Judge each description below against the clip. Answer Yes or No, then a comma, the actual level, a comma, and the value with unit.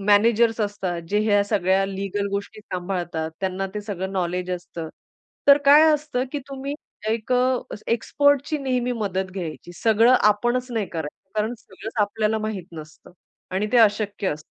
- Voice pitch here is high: Yes, high, 205 Hz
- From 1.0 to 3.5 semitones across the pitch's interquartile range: No, average, 3.9 semitones